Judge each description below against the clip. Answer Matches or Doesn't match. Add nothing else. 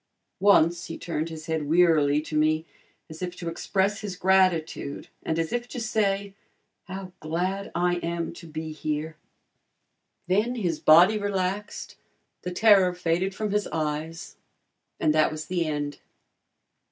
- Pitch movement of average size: Matches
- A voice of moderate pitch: Matches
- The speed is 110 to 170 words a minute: Matches